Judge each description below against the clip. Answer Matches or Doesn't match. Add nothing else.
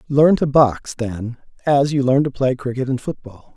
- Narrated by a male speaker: Matches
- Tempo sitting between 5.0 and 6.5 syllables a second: Doesn't match